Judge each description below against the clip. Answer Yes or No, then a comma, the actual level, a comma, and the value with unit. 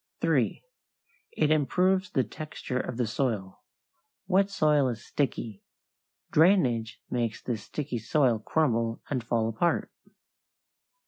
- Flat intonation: No, average, 5.2 semitones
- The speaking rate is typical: No, slow, 115 wpm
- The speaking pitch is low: Yes, low, 125 Hz